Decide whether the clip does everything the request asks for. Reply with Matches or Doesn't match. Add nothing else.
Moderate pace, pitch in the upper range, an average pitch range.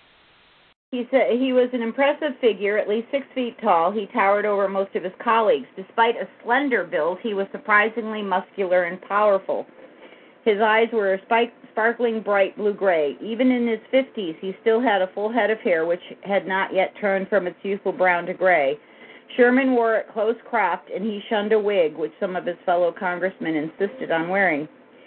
Matches